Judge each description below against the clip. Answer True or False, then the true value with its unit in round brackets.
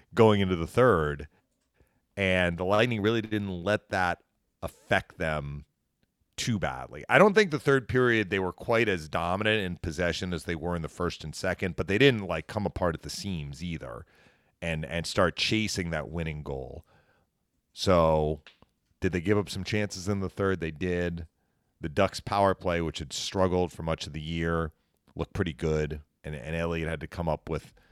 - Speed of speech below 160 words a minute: False (190 wpm)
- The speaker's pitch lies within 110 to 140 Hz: False (90 Hz)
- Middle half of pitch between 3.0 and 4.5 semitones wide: True (3.7 semitones)